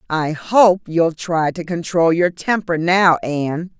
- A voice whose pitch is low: No, medium, 170 Hz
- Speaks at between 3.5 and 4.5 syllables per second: Yes, 3.8 syllables/s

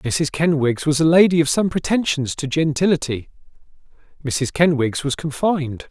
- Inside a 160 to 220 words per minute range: No, average, 140 wpm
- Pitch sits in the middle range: Yes, medium, 150 Hz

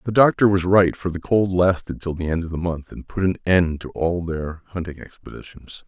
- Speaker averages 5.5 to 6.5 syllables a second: No, 5.3 syllables/s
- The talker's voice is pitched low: Yes, very low, 90 Hz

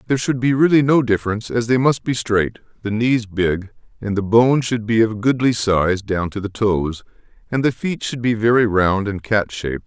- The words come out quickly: Yes, fast, 220 wpm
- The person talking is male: Yes, male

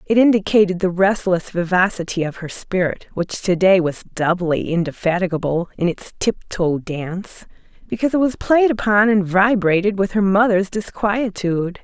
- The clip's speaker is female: Yes, female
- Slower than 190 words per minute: Yes, average, 150 wpm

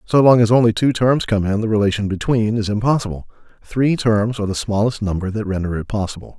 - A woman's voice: No, male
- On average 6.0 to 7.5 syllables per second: Yes, 6.2 syllables/s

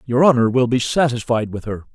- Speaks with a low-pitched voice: Yes, low, 120 Hz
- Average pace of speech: No, fast, 215 wpm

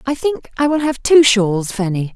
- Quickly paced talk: Yes, fast, 225 wpm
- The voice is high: Yes, high, 245 Hz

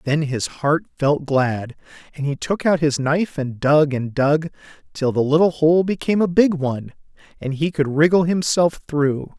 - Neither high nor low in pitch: Yes, medium, 150 Hz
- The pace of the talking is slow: No, average, 185 wpm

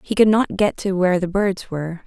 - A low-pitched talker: No, high, 190 Hz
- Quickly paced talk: Yes, fast, 260 wpm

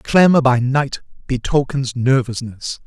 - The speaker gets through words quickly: No, slow, 105 wpm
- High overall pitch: No, low, 130 Hz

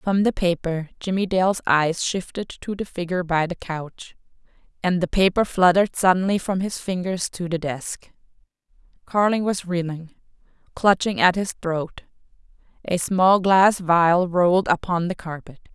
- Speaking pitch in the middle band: Yes, medium, 180 Hz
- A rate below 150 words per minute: Yes, average, 140 wpm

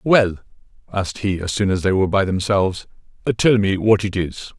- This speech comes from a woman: No, male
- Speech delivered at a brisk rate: No, average, 195 wpm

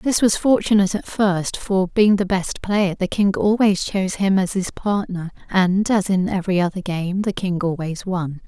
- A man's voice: No, female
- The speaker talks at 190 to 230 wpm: Yes, average, 200 wpm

